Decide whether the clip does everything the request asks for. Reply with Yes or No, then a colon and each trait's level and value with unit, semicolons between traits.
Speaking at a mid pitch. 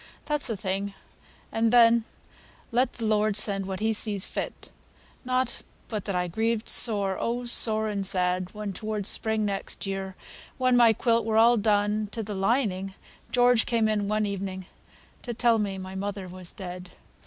No: high, 210 Hz